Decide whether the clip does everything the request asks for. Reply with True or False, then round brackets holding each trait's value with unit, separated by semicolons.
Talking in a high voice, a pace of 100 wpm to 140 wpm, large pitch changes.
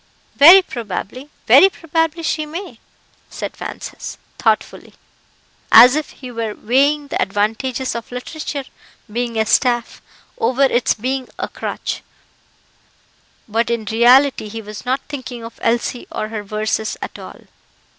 False (245 Hz; 135 wpm; 3.9 semitones)